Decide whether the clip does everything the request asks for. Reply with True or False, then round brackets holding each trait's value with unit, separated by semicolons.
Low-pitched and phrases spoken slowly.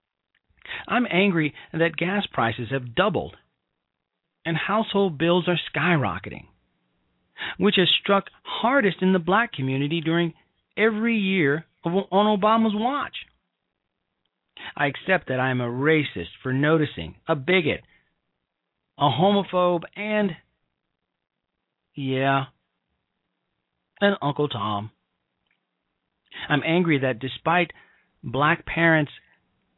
False (165 Hz; 105 wpm)